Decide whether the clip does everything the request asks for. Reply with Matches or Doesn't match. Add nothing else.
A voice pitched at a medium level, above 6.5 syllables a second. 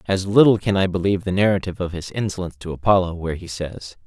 Doesn't match